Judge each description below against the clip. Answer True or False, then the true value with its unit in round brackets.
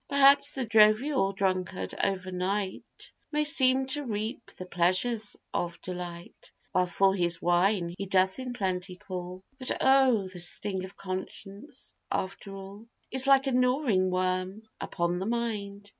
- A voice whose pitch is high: True (195 Hz)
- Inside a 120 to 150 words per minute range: True (145 wpm)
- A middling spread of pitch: True (5.0 semitones)